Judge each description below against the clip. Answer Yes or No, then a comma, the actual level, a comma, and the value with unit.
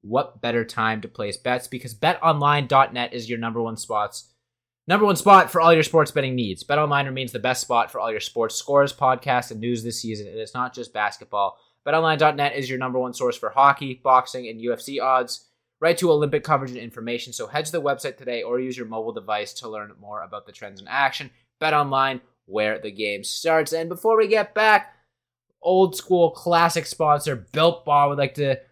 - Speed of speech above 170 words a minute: Yes, fast, 205 wpm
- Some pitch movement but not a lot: Yes, average, 4.3 semitones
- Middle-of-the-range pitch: No, low, 130 Hz